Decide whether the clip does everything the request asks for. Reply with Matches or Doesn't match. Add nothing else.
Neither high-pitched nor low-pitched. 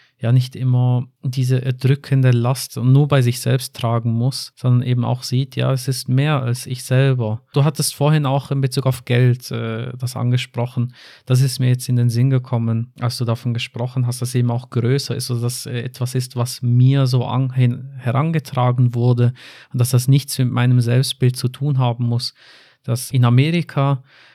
Doesn't match